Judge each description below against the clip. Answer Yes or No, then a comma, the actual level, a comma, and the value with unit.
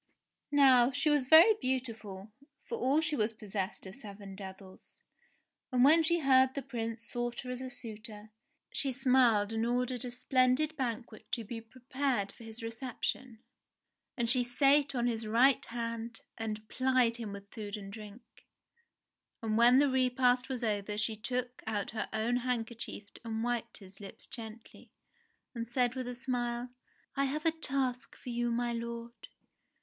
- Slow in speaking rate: No, average, 165 wpm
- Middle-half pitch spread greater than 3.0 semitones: No, average, 2.7 semitones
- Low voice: No, high, 240 Hz